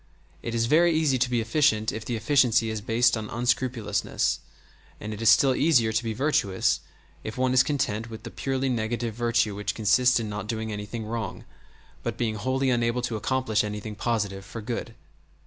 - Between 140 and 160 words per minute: No, average, 185 wpm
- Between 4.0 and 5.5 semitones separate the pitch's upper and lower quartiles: No, average, 2.7 semitones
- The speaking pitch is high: No, low, 115 Hz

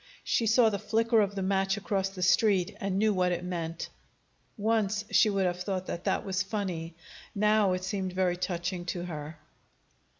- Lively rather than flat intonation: No, narrow, 2.6 semitones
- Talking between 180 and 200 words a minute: Yes, average, 185 wpm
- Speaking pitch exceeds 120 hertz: Yes, high, 190 Hz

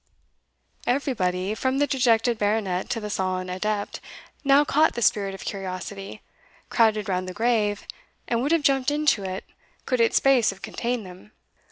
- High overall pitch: Yes, high, 215 Hz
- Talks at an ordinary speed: Yes, average, 160 wpm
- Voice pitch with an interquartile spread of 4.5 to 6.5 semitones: Yes, average, 4.8 semitones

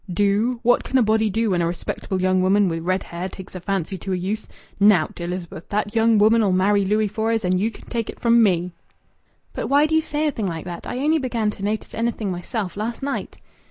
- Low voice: No, high, 205 Hz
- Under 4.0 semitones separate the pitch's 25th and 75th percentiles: Yes, average, 3.6 semitones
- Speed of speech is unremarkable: No, fast, 230 wpm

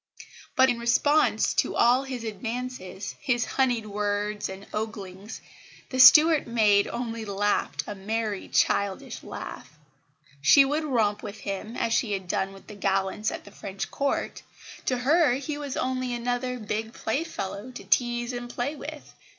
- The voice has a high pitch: Yes, high, 230 Hz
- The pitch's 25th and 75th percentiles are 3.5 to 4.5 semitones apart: Yes, average, 3.9 semitones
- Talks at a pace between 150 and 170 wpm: Yes, average, 155 wpm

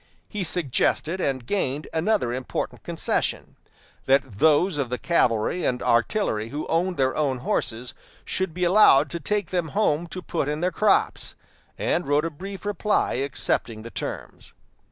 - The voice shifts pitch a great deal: Yes, wide, 5.7 semitones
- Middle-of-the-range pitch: Yes, medium, 155 Hz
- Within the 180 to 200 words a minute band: No, average, 155 wpm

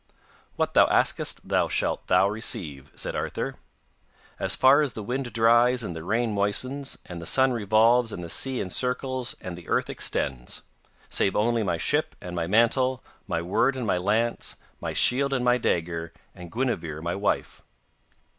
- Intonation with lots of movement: Yes, wide, 6.1 semitones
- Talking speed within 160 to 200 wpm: Yes, average, 170 wpm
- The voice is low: Yes, low, 110 Hz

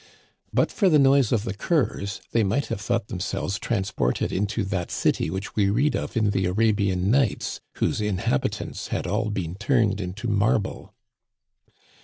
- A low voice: Yes, low, 105 Hz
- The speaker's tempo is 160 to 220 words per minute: Yes, average, 165 wpm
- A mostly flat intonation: No, average, 3.3 semitones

